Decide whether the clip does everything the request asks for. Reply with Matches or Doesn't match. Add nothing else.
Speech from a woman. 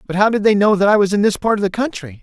Doesn't match